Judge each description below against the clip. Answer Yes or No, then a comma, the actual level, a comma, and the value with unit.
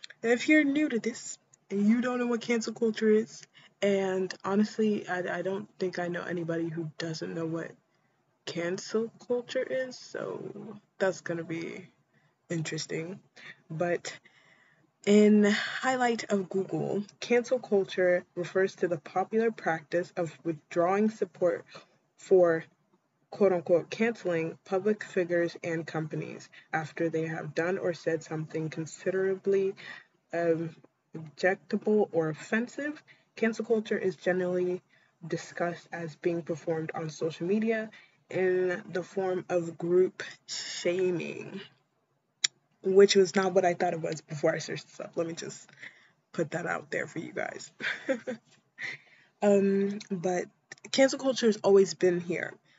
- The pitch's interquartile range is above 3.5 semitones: Yes, average, 4.0 semitones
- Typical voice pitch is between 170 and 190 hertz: Yes, medium, 185 Hz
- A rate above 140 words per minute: No, slow, 135 wpm